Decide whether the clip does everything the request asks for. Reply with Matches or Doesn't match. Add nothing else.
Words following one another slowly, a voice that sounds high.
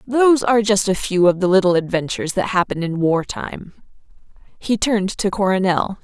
Doesn't match